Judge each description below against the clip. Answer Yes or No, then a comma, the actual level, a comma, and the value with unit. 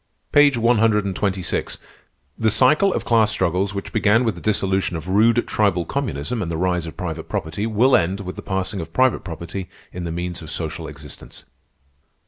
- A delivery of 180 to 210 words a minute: Yes, average, 195 wpm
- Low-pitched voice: Yes, very low, 95 Hz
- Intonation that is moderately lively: Yes, average, 4.5 semitones